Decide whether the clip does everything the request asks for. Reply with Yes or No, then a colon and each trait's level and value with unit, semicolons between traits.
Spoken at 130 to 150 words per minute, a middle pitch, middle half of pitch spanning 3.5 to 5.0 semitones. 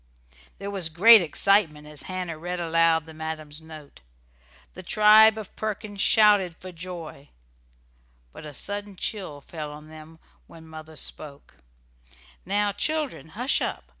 Yes: slow, 135 wpm; medium, 170 Hz; average, 4.5 semitones